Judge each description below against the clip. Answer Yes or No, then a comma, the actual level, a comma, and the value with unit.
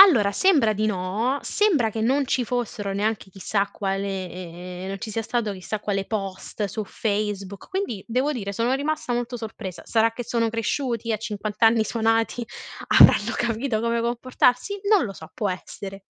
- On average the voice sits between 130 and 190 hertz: No, high, 220 Hz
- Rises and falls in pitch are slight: No, average, 3.4 semitones